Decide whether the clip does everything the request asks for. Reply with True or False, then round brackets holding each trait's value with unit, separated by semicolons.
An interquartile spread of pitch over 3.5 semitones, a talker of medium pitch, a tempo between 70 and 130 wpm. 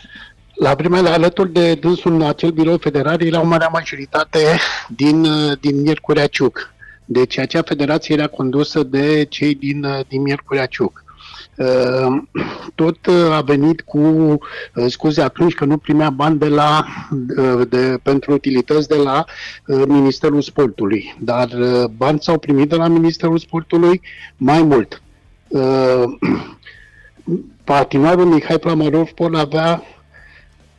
False (3.1 semitones; 150 Hz; 120 wpm)